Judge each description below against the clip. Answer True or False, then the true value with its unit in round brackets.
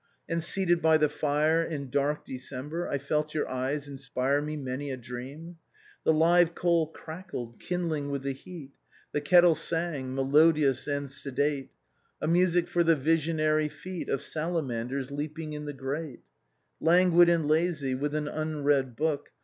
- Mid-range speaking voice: True (150 Hz)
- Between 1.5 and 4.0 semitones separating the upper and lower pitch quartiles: True (2.9 semitones)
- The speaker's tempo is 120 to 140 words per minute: False (160 wpm)